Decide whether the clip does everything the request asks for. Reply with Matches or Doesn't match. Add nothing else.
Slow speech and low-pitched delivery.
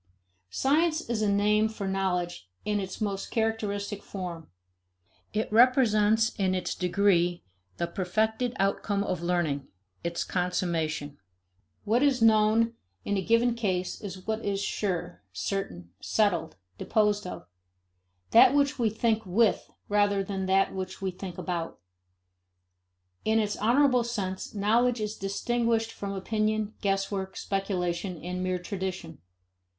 Doesn't match